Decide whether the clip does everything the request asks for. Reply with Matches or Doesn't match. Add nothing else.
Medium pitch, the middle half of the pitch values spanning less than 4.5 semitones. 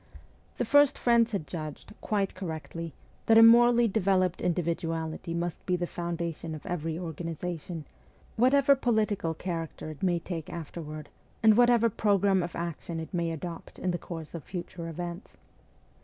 Matches